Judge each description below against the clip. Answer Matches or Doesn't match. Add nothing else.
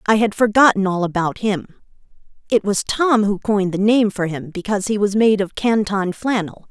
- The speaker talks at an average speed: Matches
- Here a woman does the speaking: Matches